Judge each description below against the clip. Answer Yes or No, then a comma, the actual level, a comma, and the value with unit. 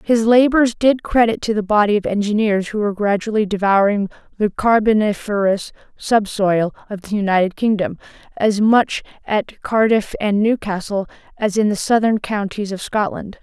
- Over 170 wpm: No, average, 150 wpm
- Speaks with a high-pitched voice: Yes, high, 205 Hz